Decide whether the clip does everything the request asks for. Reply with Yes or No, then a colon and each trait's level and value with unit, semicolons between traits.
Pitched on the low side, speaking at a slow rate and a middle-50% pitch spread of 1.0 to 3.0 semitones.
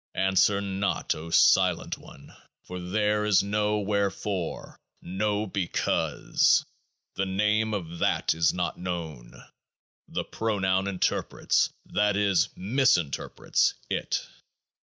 Yes: very low, 95 Hz; slow, 115 wpm; narrow, 2.6 semitones